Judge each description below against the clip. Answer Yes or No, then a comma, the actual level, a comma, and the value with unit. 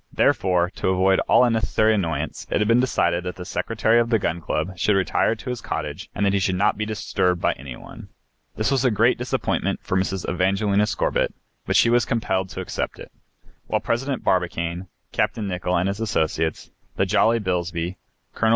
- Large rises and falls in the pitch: No, average, 3.6 semitones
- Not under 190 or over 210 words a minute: Yes, average, 195 wpm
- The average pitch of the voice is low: Yes, very low, 95 Hz